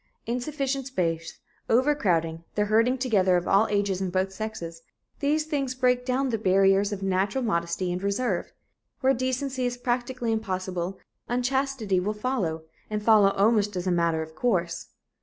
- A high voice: Yes, high, 210 Hz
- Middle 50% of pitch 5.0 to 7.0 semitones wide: Yes, average, 5.3 semitones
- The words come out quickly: No, average, 160 wpm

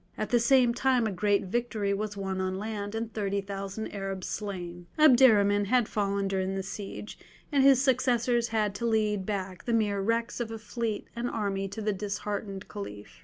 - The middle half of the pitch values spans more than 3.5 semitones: No, average, 2.9 semitones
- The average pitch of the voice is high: Yes, high, 210 Hz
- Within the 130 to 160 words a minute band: No, average, 185 wpm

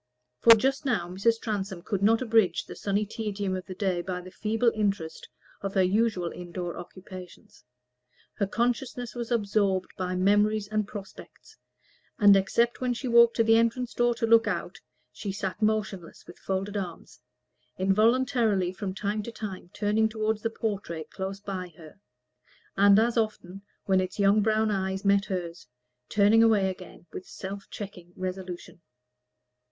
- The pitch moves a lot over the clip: No, average, 3.0 semitones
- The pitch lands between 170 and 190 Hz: No, high, 200 Hz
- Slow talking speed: No, average, 160 wpm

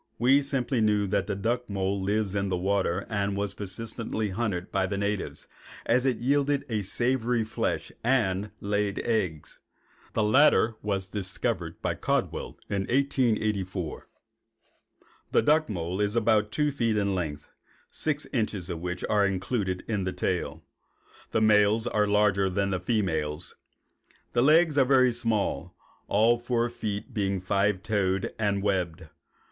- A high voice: No, low, 105 Hz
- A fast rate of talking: No, average, 150 wpm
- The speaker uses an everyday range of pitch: Yes, average, 3.5 semitones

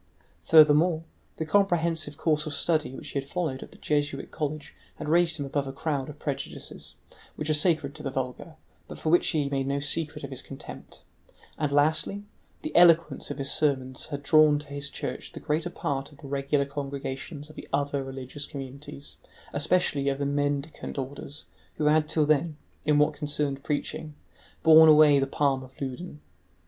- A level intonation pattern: Yes, narrow, 2.0 semitones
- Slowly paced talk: No, average, 180 wpm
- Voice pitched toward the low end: No, medium, 145 Hz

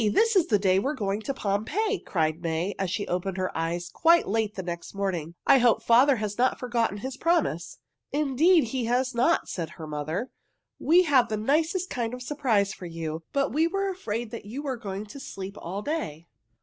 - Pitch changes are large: Yes, wide, 6.8 semitones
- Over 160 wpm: Yes, average, 200 wpm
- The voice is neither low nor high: No, high, 225 Hz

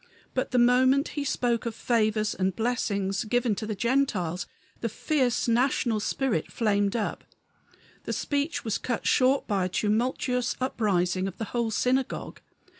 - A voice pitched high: Yes, high, 230 Hz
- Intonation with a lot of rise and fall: No, average, 3.7 semitones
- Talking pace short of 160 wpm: Yes, average, 150 wpm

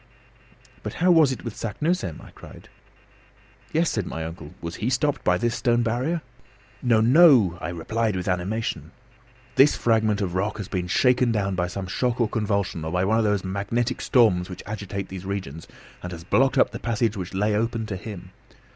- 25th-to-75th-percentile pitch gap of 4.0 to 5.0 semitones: Yes, average, 4.5 semitones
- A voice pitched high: No, low, 105 Hz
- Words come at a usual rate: Yes, average, 190 wpm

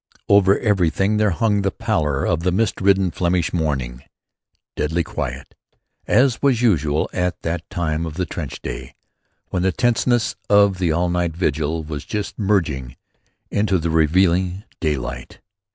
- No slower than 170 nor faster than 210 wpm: No, average, 150 wpm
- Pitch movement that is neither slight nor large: Yes, average, 4.2 semitones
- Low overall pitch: Yes, very low, 85 Hz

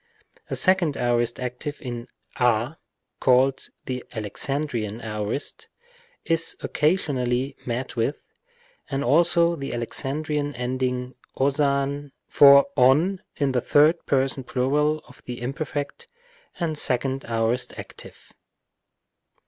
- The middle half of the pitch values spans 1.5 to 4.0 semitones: Yes, average, 3.1 semitones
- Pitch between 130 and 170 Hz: Yes, low, 135 Hz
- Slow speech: Yes, slow, 110 wpm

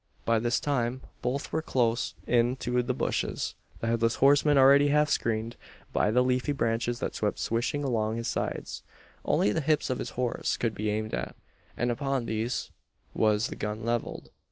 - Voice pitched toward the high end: No, low, 120 Hz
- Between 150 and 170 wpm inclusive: No, average, 180 wpm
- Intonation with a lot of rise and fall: No, average, 2.8 semitones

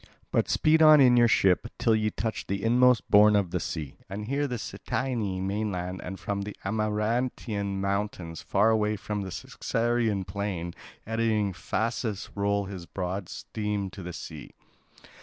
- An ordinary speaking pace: Yes, average, 160 wpm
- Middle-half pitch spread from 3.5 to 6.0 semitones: No, average, 2.7 semitones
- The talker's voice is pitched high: No, low, 105 Hz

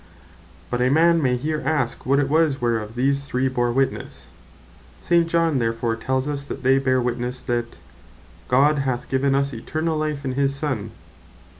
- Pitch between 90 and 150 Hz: Yes, low, 135 Hz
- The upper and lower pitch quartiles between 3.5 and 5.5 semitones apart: No, average, 3.0 semitones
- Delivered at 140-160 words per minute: No, average, 180 wpm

